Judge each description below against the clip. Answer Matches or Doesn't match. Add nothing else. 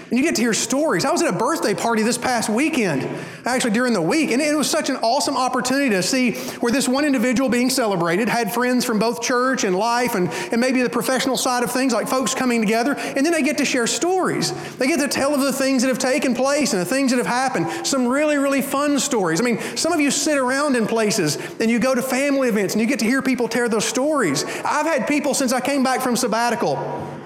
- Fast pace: Matches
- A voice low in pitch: Doesn't match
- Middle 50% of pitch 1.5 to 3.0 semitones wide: Matches